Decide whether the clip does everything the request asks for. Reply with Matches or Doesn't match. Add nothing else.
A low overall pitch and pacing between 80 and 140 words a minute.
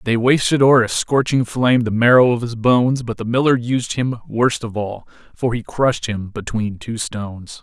Doesn't match